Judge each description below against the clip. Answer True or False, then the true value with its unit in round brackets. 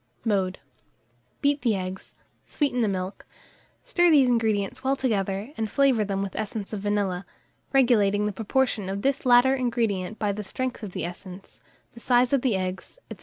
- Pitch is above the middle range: True (215 Hz)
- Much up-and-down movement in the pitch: False (4.5 semitones)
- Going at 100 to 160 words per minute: False (170 wpm)